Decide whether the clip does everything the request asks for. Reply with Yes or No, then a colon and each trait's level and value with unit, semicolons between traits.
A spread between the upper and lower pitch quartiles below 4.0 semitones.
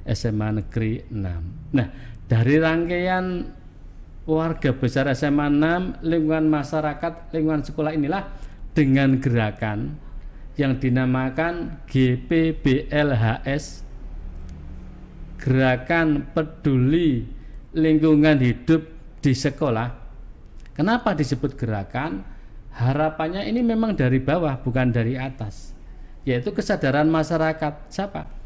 No: average, 4.3 semitones